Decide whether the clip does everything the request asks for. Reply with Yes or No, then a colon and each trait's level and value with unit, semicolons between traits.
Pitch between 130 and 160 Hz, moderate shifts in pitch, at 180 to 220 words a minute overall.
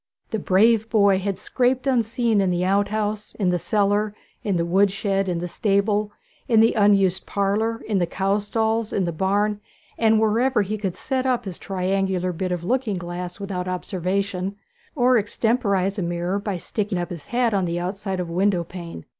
No: high, 200 Hz; average, 3.0 semitones; average, 190 wpm